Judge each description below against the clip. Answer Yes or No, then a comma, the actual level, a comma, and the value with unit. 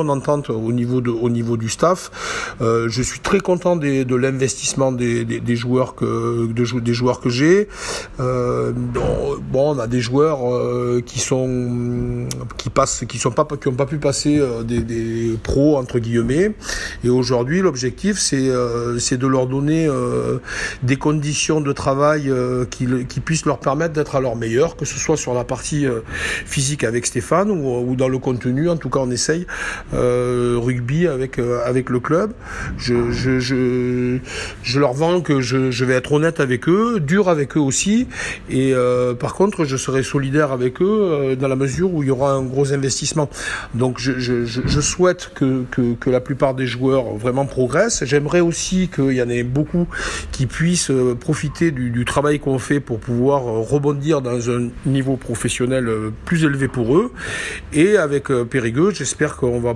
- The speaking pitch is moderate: No, low, 130 Hz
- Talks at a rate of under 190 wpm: Yes, average, 180 wpm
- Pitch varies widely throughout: No, average, 3.2 semitones